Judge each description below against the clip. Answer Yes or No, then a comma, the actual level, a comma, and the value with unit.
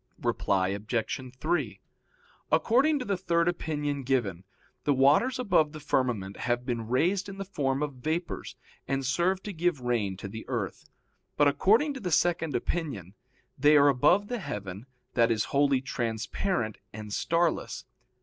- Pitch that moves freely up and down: Yes, wide, 6.8 semitones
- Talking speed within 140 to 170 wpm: Yes, average, 155 wpm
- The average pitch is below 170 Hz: Yes, medium, 140 Hz